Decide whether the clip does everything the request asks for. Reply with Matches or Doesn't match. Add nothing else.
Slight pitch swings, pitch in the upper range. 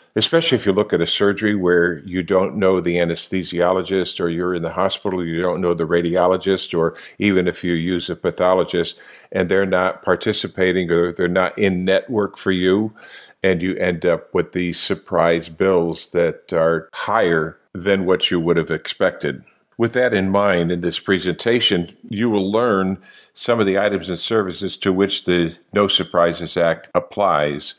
Doesn't match